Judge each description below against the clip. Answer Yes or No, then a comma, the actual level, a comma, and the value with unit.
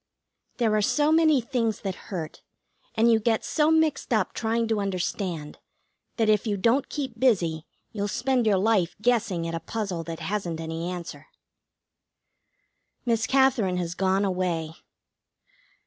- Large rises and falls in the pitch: No, average, 4.8 semitones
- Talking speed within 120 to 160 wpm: Yes, average, 150 wpm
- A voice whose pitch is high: Yes, high, 210 Hz